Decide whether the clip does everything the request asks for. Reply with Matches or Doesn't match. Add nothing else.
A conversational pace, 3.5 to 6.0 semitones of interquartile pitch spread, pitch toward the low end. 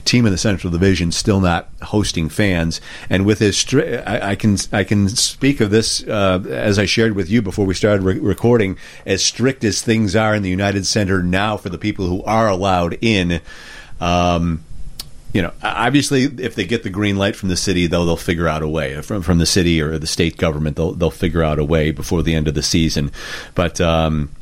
Doesn't match